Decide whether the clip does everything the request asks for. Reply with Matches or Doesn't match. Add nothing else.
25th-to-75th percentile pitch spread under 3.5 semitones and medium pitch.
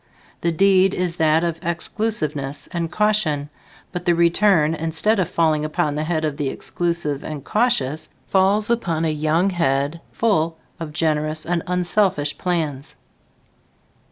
Matches